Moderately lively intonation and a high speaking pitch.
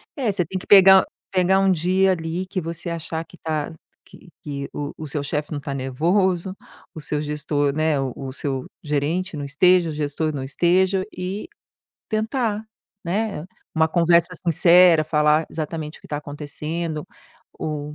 No: average, 3.7 semitones; medium, 160 Hz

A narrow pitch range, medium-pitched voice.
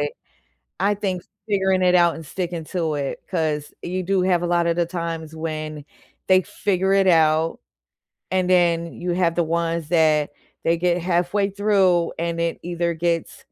Yes: narrow, 2.0 semitones; medium, 170 Hz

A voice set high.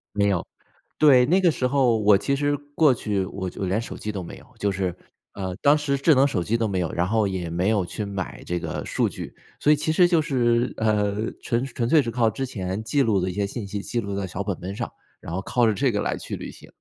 No: low, 110 Hz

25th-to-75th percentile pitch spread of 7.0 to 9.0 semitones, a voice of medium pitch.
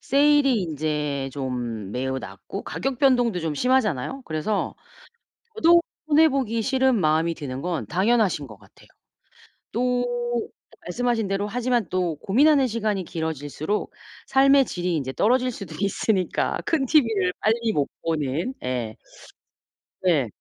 No: wide, 8.6 semitones; high, 195 Hz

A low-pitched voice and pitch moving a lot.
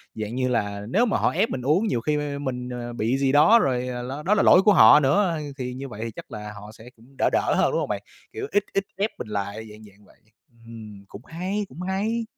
Yes: low, 130 Hz; wide, 8.5 semitones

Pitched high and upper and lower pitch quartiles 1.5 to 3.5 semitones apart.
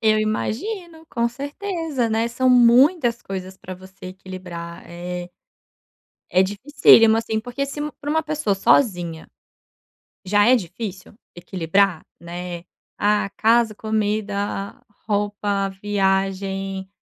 No: high, 205 Hz; average, 4.1 semitones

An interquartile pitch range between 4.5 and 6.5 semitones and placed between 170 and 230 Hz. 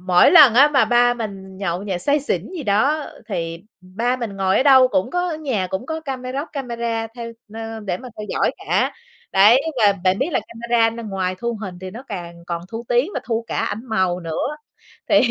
Yes: average, 5.1 semitones; high, 225 Hz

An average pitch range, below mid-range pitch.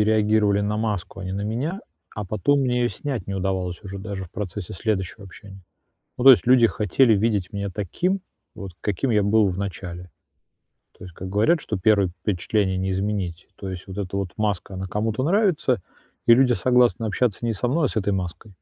Yes: average, 3.3 semitones; low, 105 Hz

